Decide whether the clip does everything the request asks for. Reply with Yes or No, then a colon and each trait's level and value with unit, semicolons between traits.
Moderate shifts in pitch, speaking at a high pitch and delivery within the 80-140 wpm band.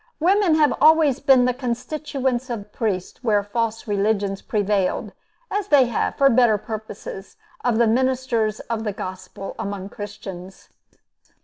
Yes: average, 4.3 semitones; high, 230 Hz; slow, 135 wpm